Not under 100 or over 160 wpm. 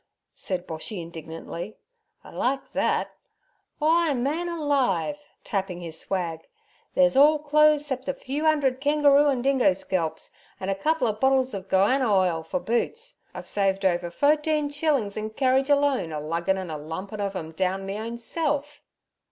Yes: average, 155 wpm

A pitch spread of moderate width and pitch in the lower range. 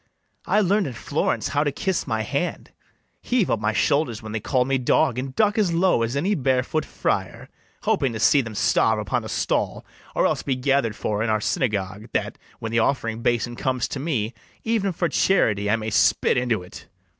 No: wide, 5.8 semitones; low, 125 Hz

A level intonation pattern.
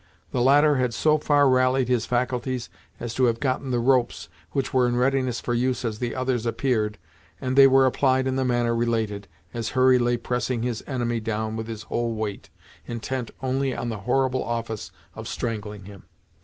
Yes: narrow, 2.1 semitones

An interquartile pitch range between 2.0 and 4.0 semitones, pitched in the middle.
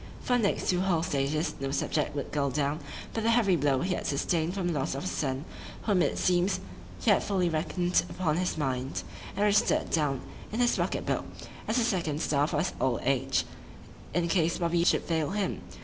No: average, 4.5 semitones; medium, 170 Hz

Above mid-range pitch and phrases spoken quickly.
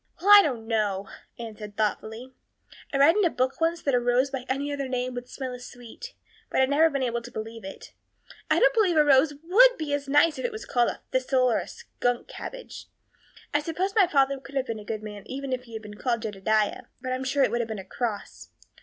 Yes: very high, 260 Hz; fast, 245 wpm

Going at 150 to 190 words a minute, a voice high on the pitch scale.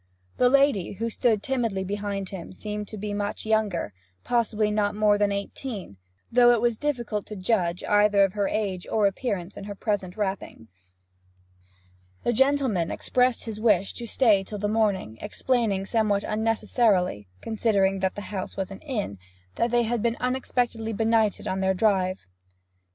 Yes: average, 160 wpm; high, 210 Hz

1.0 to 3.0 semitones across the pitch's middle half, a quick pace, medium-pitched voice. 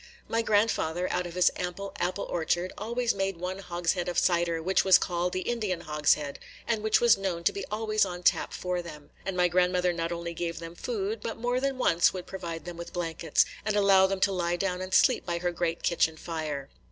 Yes: narrow, 2.5 semitones; fast, 215 wpm; medium, 180 Hz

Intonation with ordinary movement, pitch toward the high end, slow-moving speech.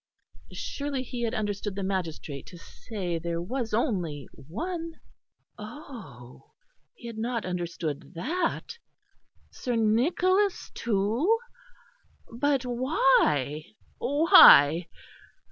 No: wide, 7.8 semitones; high, 220 Hz; slow, 95 wpm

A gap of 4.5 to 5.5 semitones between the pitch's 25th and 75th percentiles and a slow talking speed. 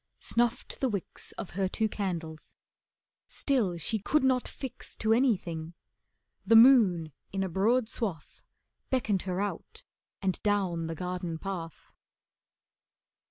Yes: average, 4.8 semitones; slow, 125 wpm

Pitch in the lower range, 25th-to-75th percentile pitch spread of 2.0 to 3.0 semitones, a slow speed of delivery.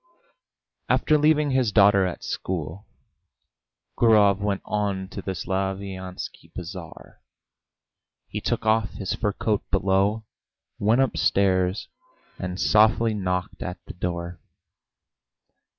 Yes: low, 100 Hz; average, 2.7 semitones; slow, 105 wpm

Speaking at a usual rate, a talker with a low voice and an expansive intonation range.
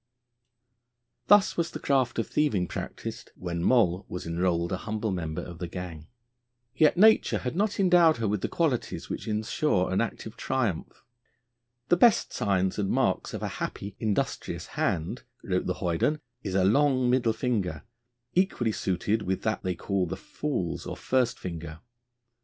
Yes: average, 160 wpm; low, 105 Hz; wide, 6.5 semitones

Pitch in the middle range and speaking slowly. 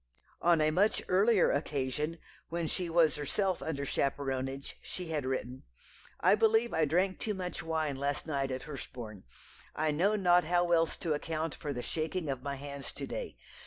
No: medium, 155 Hz; average, 175 wpm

